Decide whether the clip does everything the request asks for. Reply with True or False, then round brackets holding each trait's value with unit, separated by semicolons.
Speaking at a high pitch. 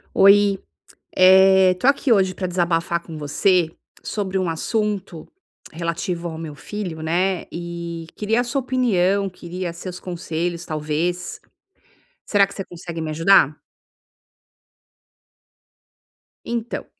False (180 Hz)